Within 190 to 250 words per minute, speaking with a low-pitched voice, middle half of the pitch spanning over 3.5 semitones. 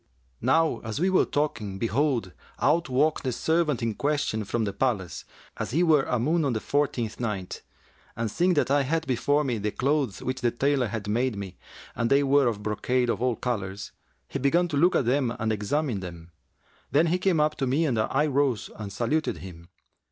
Yes: fast, 205 wpm; low, 130 Hz; average, 5.2 semitones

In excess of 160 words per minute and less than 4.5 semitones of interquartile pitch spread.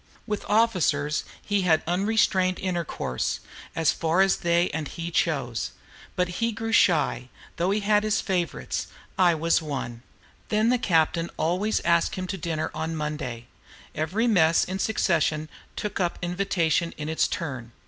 No: average, 150 wpm; average, 3.9 semitones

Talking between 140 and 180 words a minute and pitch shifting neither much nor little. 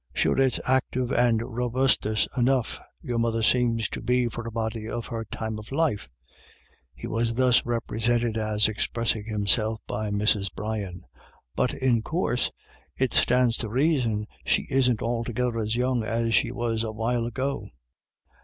No: average, 170 wpm; narrow, 2.1 semitones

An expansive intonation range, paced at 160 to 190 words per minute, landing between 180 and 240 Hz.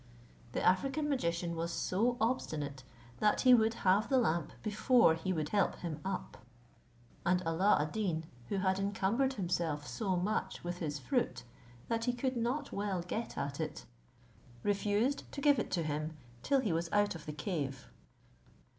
Yes: wide, 5.9 semitones; average, 165 wpm; high, 190 Hz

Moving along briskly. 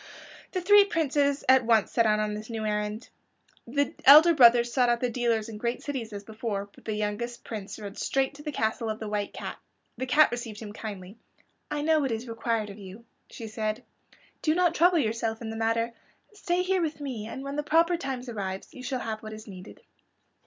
Yes: fast, 215 wpm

